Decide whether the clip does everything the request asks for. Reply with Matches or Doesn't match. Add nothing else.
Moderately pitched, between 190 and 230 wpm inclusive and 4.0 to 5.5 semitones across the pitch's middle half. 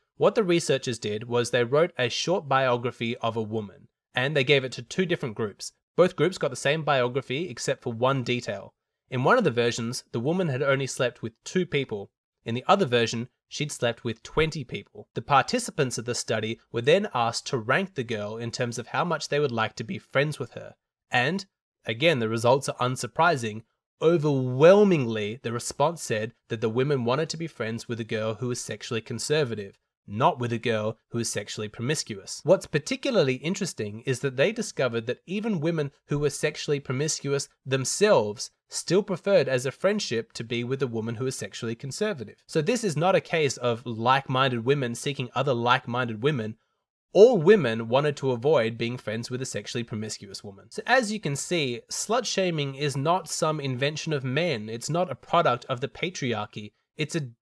Doesn't match